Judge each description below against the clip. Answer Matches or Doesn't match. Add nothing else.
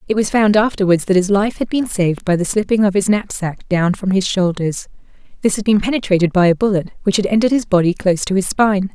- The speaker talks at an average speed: Doesn't match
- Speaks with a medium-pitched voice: Doesn't match